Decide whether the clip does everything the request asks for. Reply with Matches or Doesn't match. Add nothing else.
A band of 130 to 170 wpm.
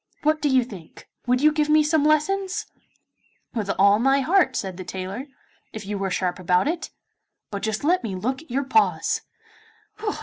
Doesn't match